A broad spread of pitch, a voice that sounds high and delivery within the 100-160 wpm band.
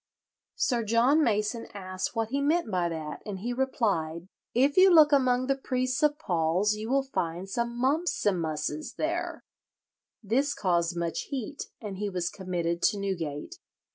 Yes: wide, 6.9 semitones; high, 215 Hz; average, 155 wpm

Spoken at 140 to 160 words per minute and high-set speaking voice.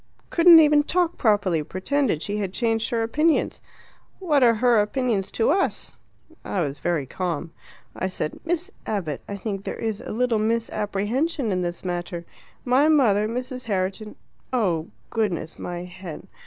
Yes: average, 155 wpm; high, 215 Hz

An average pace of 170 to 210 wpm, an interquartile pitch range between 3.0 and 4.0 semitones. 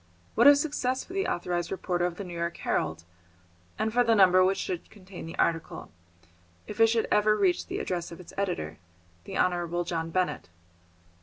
Yes: average, 185 wpm; average, 3.7 semitones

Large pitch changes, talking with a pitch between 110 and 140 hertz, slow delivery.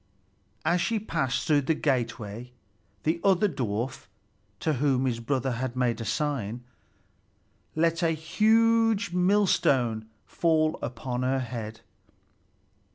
Yes: wide, 5.7 semitones; low, 135 Hz; slow, 115 wpm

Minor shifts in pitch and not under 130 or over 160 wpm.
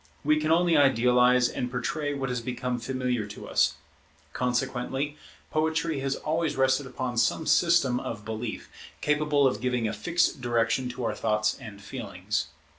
No: average, 3.8 semitones; average, 155 wpm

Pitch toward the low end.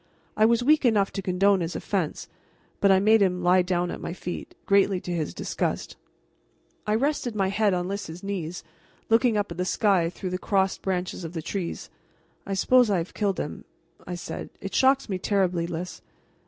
No: high, 195 Hz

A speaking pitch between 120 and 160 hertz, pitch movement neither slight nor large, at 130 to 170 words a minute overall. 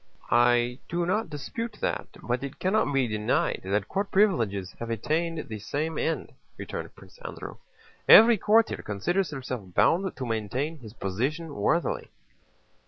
No: medium, 140 Hz; wide, 7.5 semitones; average, 145 wpm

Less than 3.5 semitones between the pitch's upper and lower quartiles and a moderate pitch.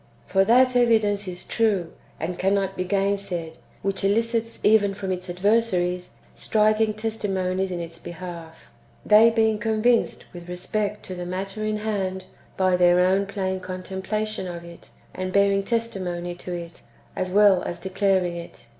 No: average, 2.9 semitones; high, 195 Hz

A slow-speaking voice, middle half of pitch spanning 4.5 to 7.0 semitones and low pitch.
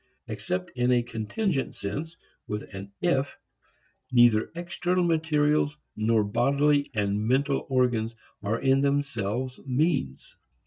Yes: slow, 115 wpm; average, 5.2 semitones; low, 130 Hz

